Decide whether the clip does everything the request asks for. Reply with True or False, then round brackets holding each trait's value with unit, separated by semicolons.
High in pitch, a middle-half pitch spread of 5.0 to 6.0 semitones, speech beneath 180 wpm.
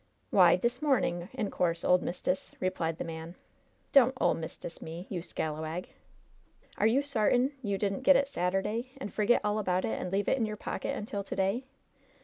False (200 Hz; 5.3 semitones; 190 wpm)